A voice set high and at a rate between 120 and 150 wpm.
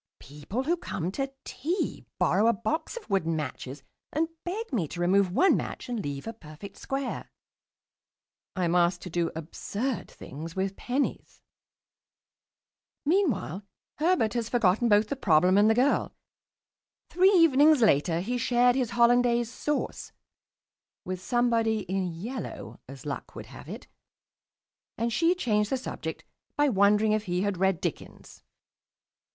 Yes: high, 215 Hz; average, 145 wpm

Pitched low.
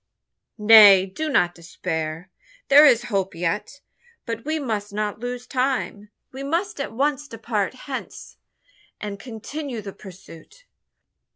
No: high, 225 Hz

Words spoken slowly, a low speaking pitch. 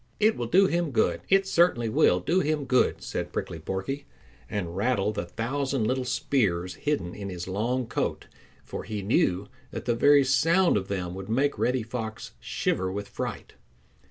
No: average, 175 wpm; low, 115 Hz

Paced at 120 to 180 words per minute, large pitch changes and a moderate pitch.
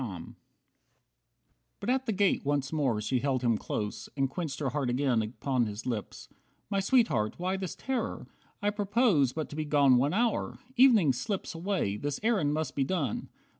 Yes: average, 175 wpm; wide, 7.6 semitones; medium, 145 Hz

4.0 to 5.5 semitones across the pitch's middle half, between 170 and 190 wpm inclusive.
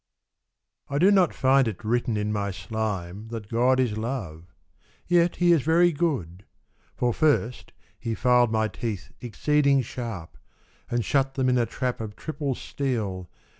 No: average, 4.5 semitones; average, 155 wpm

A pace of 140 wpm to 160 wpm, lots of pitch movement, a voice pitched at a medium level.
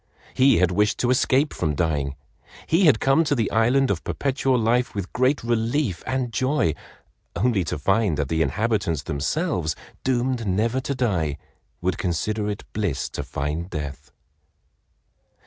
No: average, 150 wpm; wide, 7.4 semitones; low, 110 Hz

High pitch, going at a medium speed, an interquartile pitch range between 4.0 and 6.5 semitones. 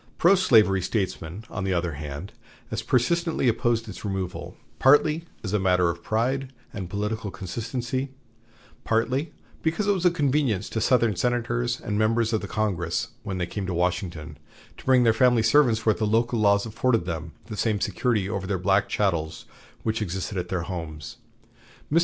No: low, 110 Hz; average, 170 wpm; average, 4.7 semitones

